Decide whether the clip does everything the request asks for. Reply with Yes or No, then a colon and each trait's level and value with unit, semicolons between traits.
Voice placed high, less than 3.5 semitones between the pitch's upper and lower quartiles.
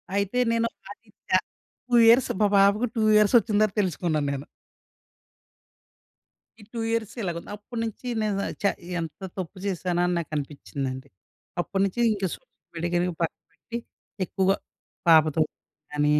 No: high, 195 Hz; average, 4.6 semitones